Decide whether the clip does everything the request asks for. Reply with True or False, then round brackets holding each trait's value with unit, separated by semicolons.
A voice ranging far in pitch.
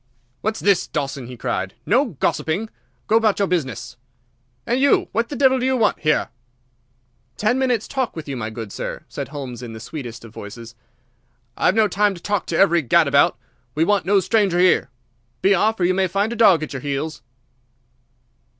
True (8.1 semitones)